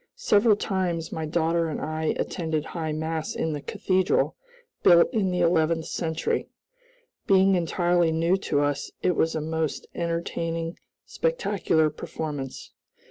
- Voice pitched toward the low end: No, medium, 165 Hz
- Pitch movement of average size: No, narrow, 2.2 semitones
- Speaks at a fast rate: No, slow, 135 wpm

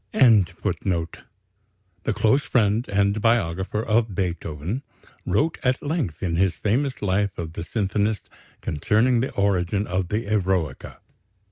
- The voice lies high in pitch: No, low, 100 Hz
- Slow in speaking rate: Yes, slow, 130 wpm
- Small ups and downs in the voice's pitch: No, average, 3.8 semitones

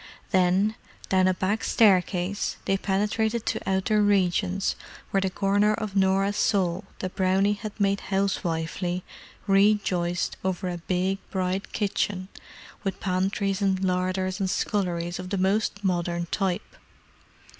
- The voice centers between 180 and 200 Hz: Yes, high, 190 Hz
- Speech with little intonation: Yes, narrow, 1.7 semitones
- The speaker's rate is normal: No, slow, 130 wpm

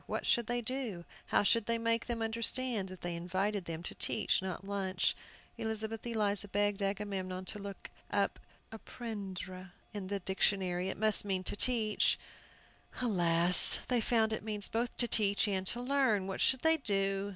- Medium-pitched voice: No, high, 205 Hz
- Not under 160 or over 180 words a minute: Yes, average, 170 wpm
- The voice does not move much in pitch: No, average, 3.2 semitones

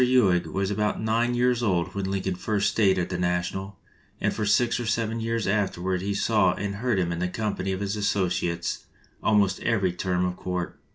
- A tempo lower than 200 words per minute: No, fast, 205 wpm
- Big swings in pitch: No, average, 3.2 semitones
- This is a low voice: Yes, low, 100 Hz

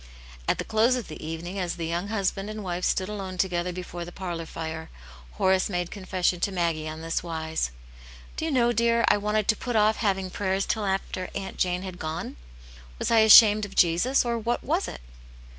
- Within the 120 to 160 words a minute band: No, fast, 205 wpm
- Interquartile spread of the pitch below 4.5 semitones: Yes, average, 3.6 semitones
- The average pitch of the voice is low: No, medium, 185 Hz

